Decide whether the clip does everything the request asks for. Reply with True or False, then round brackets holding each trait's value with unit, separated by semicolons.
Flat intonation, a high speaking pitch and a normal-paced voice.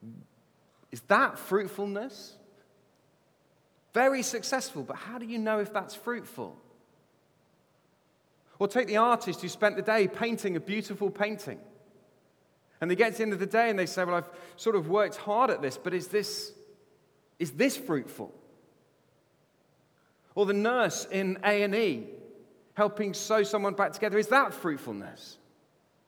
True (2.3 semitones; 205 Hz; 150 wpm)